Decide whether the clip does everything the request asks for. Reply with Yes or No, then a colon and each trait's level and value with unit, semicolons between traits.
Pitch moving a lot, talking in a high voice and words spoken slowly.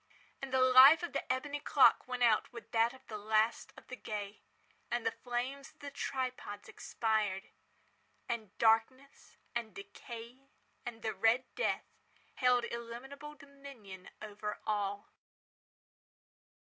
No: average, 3.5 semitones; high, 240 Hz; slow, 130 wpm